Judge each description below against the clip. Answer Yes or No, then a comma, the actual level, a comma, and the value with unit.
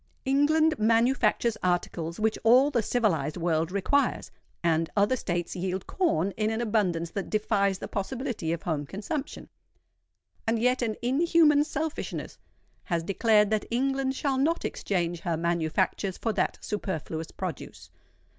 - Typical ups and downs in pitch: No, wide, 6.9 semitones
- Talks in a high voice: Yes, high, 215 Hz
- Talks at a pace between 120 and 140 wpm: Yes, slow, 135 wpm